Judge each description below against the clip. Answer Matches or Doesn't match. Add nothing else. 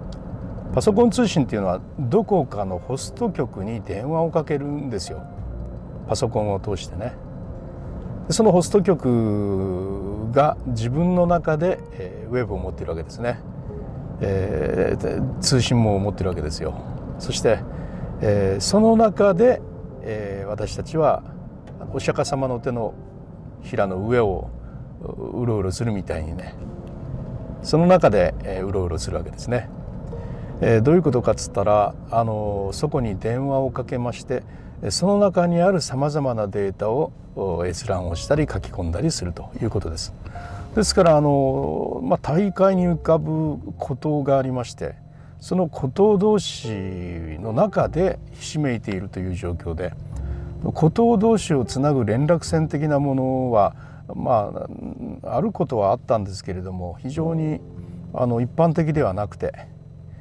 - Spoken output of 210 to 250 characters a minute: Doesn't match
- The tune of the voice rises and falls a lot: Matches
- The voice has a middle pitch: Doesn't match